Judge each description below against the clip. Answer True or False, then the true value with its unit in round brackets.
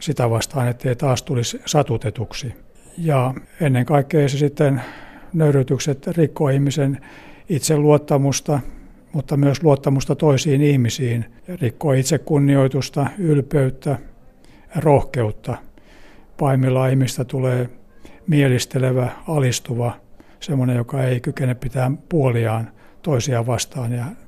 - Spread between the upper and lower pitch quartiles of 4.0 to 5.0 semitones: False (2.8 semitones)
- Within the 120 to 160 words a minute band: False (95 wpm)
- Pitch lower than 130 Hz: False (135 Hz)